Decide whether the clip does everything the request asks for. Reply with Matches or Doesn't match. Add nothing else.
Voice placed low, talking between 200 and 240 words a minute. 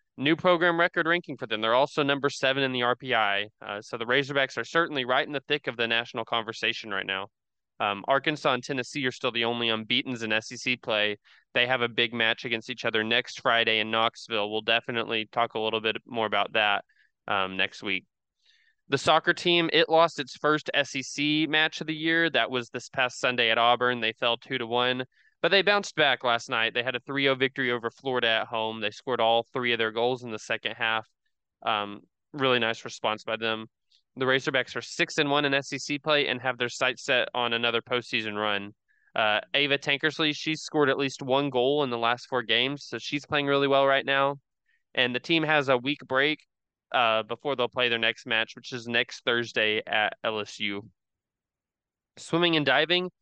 Matches